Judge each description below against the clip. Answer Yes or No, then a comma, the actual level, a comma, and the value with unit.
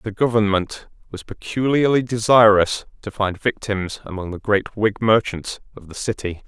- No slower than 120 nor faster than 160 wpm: Yes, average, 150 wpm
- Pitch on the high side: No, low, 105 Hz